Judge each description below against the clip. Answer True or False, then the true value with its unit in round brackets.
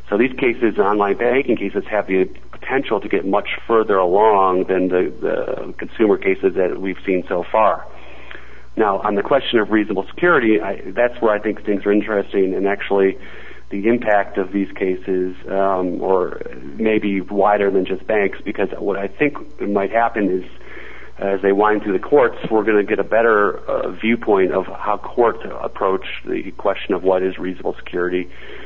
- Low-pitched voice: True (100 Hz)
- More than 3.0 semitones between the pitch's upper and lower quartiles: False (2.4 semitones)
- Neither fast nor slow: True (180 wpm)